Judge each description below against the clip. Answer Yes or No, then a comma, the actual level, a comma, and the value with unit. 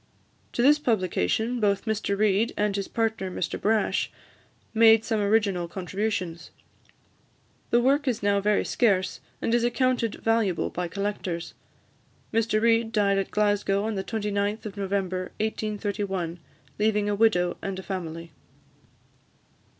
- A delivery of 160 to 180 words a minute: No, slow, 135 wpm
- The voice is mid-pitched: No, high, 205 Hz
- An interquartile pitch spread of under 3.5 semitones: Yes, narrow, 2.6 semitones